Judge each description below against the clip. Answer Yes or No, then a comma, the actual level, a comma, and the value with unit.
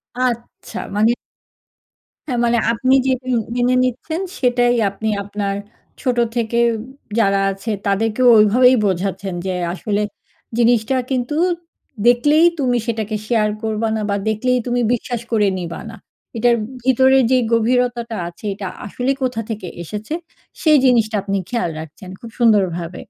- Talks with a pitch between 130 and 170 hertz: No, high, 230 Hz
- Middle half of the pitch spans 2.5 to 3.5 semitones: Yes, average, 3.2 semitones